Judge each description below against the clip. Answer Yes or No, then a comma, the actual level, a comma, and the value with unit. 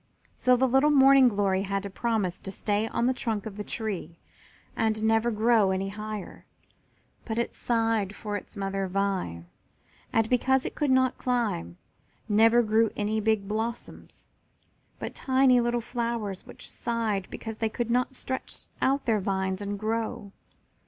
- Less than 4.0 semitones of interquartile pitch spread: Yes, average, 3.1 semitones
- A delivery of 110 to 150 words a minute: No, average, 160 wpm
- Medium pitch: No, high, 220 Hz